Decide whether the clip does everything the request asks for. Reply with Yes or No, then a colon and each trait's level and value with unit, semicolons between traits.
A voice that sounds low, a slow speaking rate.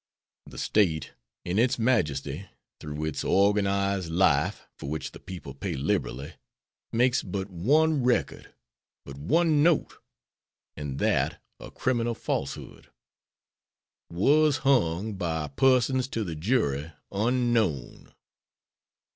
Yes: low, 100 Hz; slow, 110 wpm